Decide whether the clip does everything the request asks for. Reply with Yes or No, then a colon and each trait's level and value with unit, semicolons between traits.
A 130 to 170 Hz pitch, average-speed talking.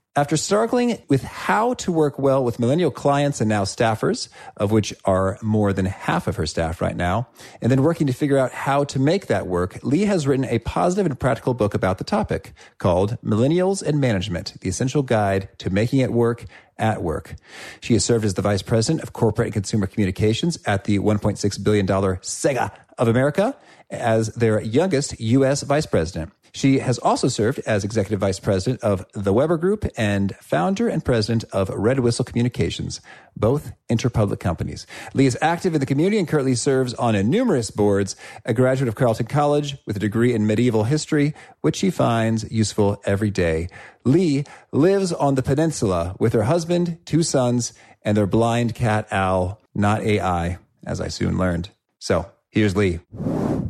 No: low, 115 Hz; average, 180 wpm